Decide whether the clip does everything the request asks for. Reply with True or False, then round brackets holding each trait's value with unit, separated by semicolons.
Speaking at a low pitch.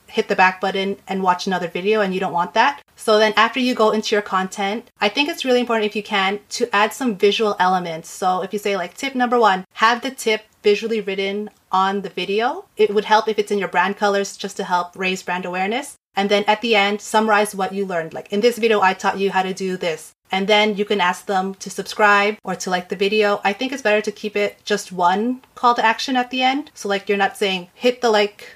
False (205 Hz)